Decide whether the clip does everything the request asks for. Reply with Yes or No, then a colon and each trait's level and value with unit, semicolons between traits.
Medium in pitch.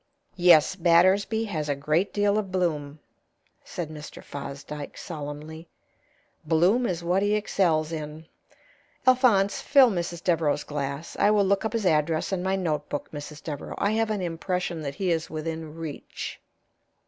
Yes: medium, 170 Hz